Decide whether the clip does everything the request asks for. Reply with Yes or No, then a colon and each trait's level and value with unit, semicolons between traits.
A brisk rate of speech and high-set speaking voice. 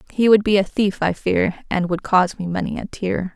Yes: fast, 250 wpm; high, 195 Hz